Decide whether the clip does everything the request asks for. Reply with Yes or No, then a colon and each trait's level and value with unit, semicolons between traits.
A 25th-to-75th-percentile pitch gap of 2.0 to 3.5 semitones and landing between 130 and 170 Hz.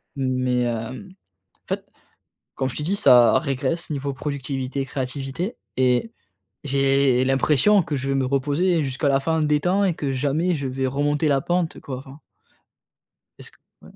Yes: average, 2.9 semitones; medium, 140 Hz